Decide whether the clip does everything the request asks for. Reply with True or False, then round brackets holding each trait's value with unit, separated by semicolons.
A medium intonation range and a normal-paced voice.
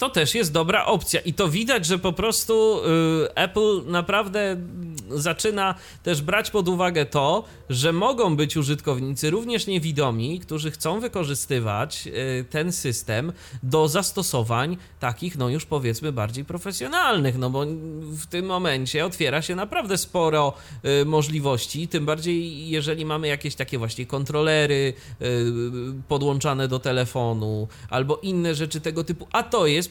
True (4.5 semitones; 140 wpm)